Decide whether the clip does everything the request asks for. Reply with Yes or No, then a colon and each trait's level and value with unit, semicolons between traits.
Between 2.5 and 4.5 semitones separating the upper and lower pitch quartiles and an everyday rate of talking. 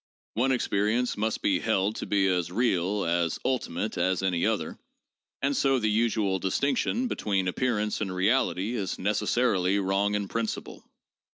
Yes: average, 3.5 semitones; average, 155 wpm